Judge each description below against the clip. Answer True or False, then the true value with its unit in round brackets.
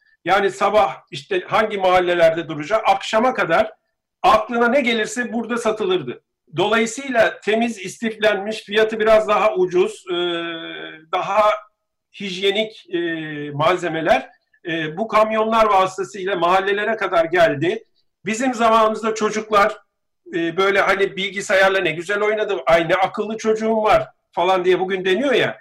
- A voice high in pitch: True (210 Hz)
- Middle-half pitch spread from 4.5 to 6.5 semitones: False (2.9 semitones)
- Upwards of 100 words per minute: True (110 wpm)